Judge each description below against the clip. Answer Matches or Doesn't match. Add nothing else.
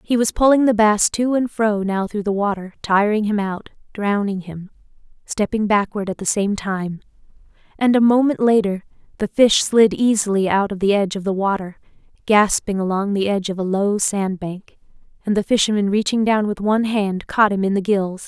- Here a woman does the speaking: Matches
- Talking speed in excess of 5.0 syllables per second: Matches